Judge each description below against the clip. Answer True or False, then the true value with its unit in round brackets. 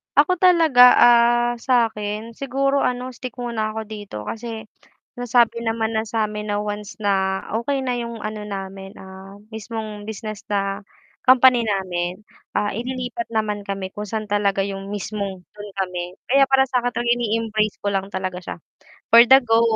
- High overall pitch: True (215 Hz)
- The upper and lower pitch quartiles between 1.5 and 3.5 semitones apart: True (3.0 semitones)